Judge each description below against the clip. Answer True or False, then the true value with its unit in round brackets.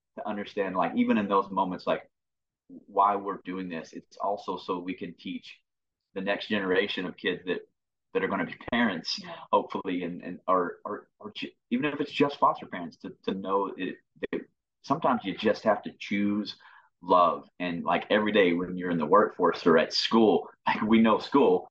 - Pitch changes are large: True (8.0 semitones)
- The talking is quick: False (190 wpm)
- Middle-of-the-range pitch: False (100 Hz)